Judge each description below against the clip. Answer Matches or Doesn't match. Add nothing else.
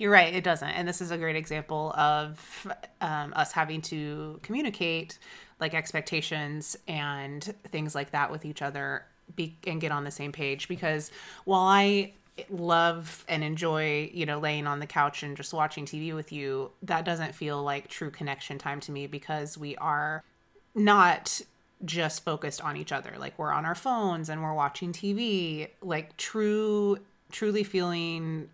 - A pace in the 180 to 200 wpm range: Doesn't match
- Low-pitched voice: Doesn't match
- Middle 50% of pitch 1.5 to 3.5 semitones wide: Matches